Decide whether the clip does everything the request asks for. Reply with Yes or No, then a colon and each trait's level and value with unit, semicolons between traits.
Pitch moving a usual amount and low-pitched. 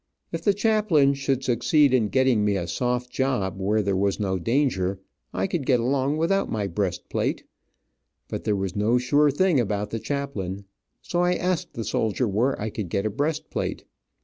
No: wide, 5.9 semitones; low, 125 Hz